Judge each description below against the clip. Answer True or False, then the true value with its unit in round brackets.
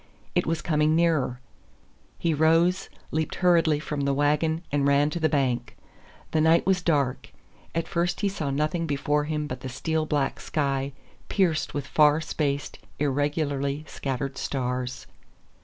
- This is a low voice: False (150 Hz)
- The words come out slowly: False (150 wpm)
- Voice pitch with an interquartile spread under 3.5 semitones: True (2.5 semitones)